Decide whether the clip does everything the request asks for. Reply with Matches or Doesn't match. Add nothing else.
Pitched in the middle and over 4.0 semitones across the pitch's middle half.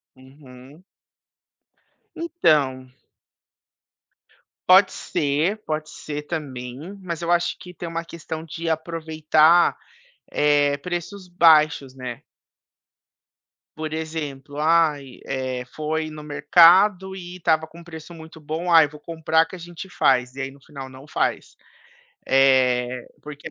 Doesn't match